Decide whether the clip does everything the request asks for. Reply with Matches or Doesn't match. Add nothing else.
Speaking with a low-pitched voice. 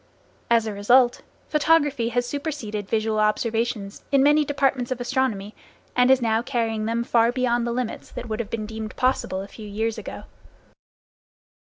Doesn't match